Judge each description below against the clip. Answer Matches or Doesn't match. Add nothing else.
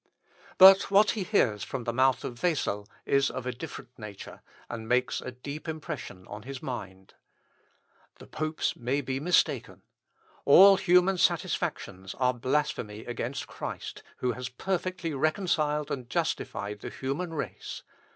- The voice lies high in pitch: Doesn't match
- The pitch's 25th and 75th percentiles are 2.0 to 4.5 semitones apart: Doesn't match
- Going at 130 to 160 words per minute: Matches